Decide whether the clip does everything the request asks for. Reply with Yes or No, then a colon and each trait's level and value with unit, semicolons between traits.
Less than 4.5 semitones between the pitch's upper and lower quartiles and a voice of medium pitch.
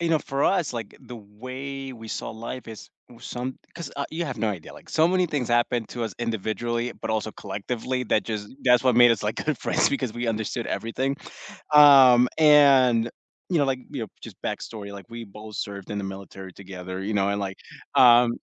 No: average, 3.7 semitones; low, 120 Hz